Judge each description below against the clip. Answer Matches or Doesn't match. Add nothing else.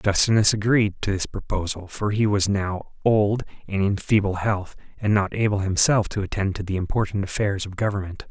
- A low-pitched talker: Matches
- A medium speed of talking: Matches